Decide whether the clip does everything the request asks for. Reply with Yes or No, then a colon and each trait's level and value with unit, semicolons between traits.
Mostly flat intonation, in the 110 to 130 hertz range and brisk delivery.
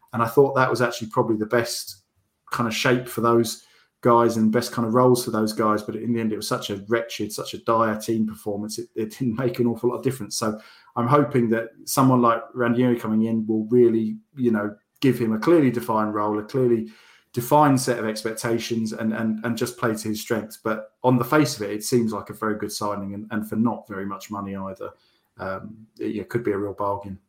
Yes: narrow, 2.0 semitones; low, 115 Hz; fast, 235 wpm